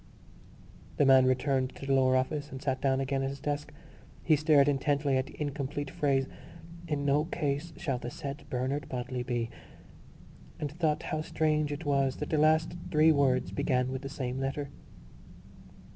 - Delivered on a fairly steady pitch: Yes, narrow, 2.0 semitones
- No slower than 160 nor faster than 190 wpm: Yes, average, 175 wpm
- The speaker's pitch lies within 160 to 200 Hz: No, medium, 140 Hz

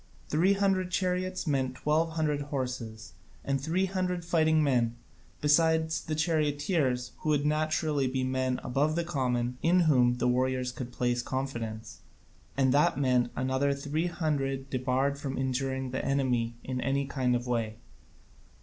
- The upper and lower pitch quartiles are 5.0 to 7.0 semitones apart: No, average, 3.7 semitones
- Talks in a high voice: No, low, 135 Hz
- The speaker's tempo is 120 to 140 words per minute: No, average, 150 wpm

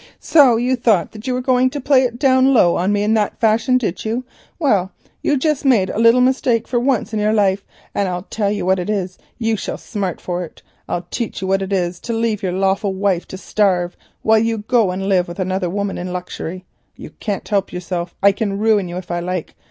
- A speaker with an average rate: No, fast, 235 wpm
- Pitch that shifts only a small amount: No, average, 3.9 semitones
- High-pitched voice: Yes, high, 205 Hz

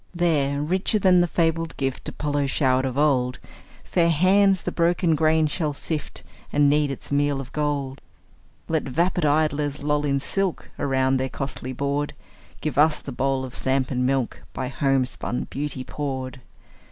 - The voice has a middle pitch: Yes, medium, 145 Hz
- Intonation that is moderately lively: Yes, average, 3.0 semitones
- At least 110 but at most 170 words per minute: Yes, average, 160 wpm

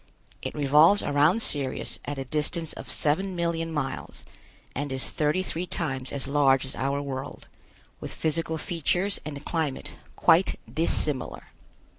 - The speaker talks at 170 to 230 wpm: No, average, 140 wpm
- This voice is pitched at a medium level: Yes, medium, 150 Hz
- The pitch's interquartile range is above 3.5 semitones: No, average, 3.1 semitones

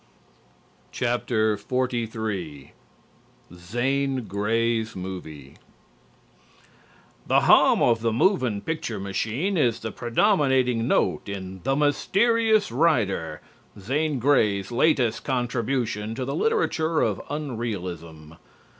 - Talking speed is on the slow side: Yes, slow, 90 wpm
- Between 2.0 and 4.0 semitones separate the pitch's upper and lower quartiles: No, wide, 5.5 semitones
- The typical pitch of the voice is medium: No, low, 120 Hz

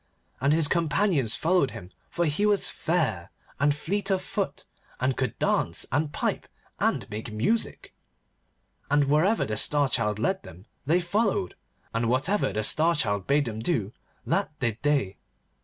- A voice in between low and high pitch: Yes, medium, 145 Hz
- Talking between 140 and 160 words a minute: Yes, average, 155 wpm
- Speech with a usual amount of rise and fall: No, wide, 7.4 semitones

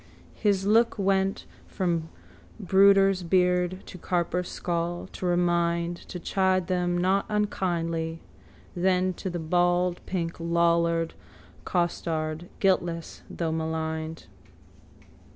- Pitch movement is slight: Yes, narrow, 1.9 semitones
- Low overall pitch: No, medium, 175 Hz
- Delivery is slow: Yes, slow, 100 wpm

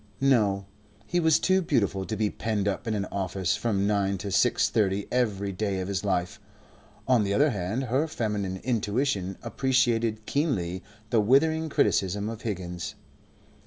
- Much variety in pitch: No, average, 4.0 semitones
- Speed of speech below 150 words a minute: No, average, 160 wpm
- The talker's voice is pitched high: No, low, 105 Hz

